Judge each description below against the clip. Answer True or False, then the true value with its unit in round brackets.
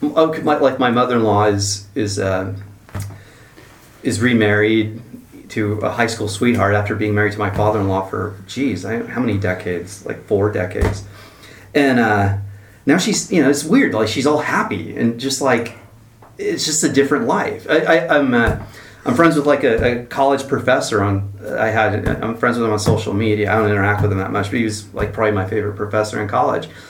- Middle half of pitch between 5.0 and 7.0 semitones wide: False (2.9 semitones)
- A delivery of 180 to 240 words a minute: True (200 wpm)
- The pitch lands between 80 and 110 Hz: True (105 Hz)